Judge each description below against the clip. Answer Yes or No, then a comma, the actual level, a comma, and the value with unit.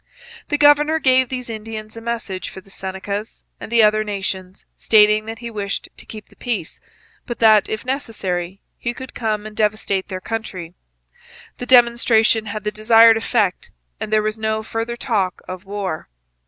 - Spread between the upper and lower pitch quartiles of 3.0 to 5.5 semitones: No, narrow, 2.6 semitones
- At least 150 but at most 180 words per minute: Yes, average, 170 wpm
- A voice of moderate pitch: No, high, 215 Hz